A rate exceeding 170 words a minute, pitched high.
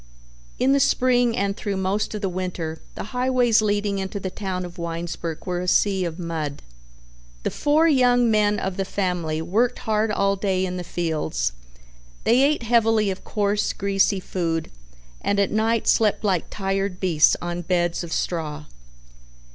No: average, 165 wpm; high, 195 Hz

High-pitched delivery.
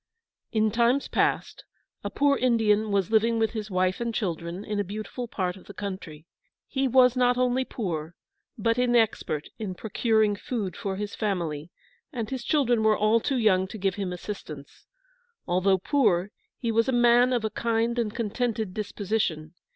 Yes: high, 215 Hz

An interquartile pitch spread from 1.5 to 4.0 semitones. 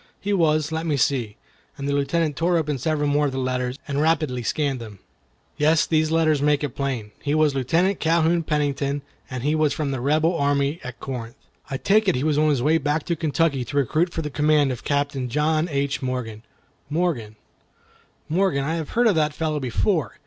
Yes: average, 2.9 semitones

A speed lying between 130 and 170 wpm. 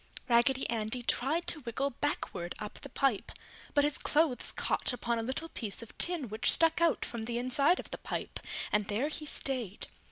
No: average, 190 wpm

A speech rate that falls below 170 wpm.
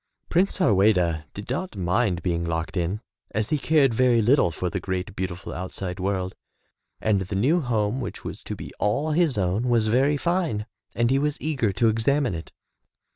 No: average, 180 wpm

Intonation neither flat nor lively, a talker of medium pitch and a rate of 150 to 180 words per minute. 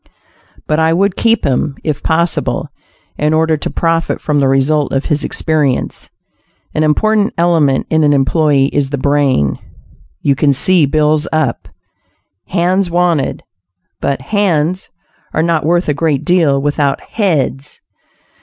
No: average, 3.2 semitones; medium, 155 Hz; average, 140 wpm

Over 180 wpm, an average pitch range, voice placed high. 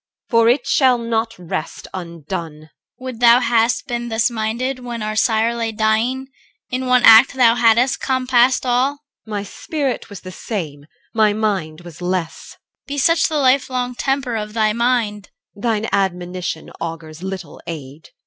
No: average, 170 wpm; average, 4.9 semitones; high, 225 Hz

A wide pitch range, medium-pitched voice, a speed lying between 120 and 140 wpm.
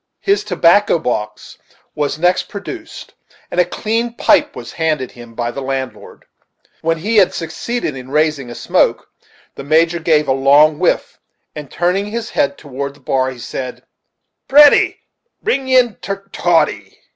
No: wide, 7.0 semitones; medium, 160 Hz; average, 155 wpm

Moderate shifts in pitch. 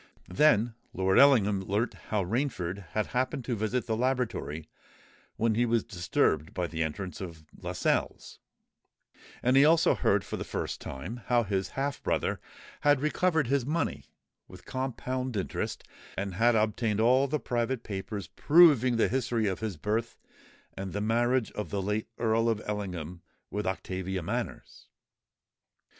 Yes: average, 4.9 semitones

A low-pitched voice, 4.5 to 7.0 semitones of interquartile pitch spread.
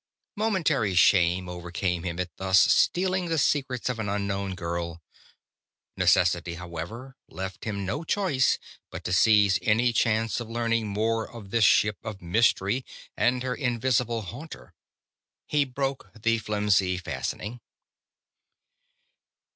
Yes: low, 110 Hz; average, 5.2 semitones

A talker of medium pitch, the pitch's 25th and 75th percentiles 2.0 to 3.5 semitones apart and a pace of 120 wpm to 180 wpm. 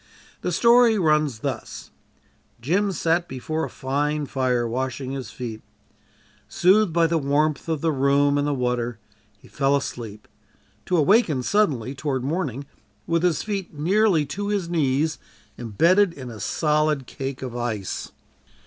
No: medium, 145 Hz; average, 4.6 semitones; average, 145 wpm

